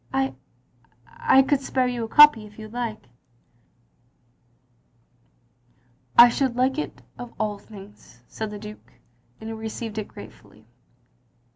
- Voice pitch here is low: No, high, 215 Hz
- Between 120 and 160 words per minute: Yes, average, 145 wpm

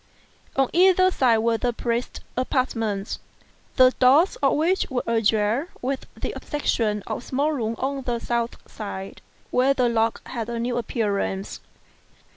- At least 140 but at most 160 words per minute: Yes, average, 150 wpm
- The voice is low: No, high, 240 Hz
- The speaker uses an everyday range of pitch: Yes, average, 3.2 semitones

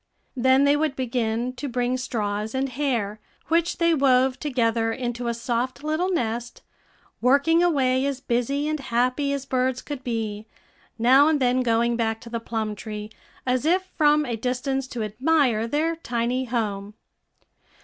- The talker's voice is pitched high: Yes, very high, 255 Hz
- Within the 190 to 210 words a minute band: No, average, 160 wpm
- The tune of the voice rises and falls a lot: No, average, 3.3 semitones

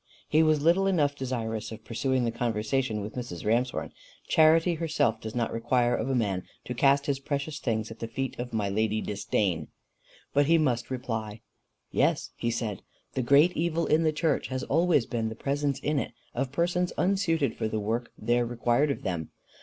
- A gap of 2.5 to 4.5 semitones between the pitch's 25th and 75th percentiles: No, average, 4.9 semitones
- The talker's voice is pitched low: Yes, low, 125 Hz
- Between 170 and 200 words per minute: Yes, average, 190 wpm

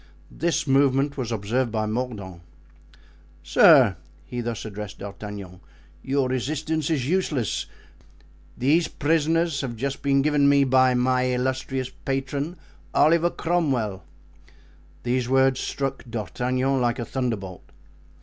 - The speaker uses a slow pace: Yes, slow, 115 wpm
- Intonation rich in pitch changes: No, average, 3.2 semitones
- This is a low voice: Yes, low, 130 Hz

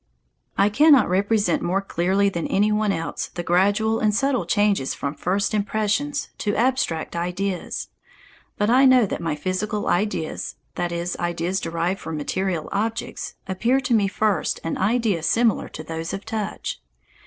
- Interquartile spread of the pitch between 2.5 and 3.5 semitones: No, average, 3.9 semitones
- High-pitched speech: Yes, high, 200 Hz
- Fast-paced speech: No, average, 155 wpm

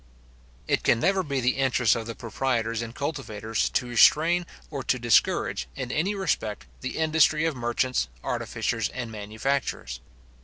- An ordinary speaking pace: Yes, average, 150 wpm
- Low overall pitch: Yes, low, 125 Hz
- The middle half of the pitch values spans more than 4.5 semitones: Yes, average, 4.9 semitones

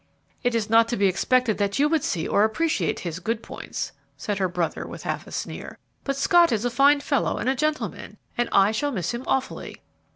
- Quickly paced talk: Yes, fast, 220 wpm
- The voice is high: Yes, high, 235 Hz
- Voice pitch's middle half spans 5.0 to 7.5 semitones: Yes, wide, 5.4 semitones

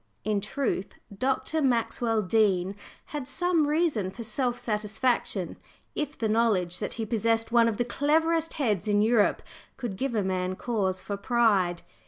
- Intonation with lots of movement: No, average, 4.4 semitones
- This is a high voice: Yes, high, 225 Hz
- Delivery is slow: No, average, 155 wpm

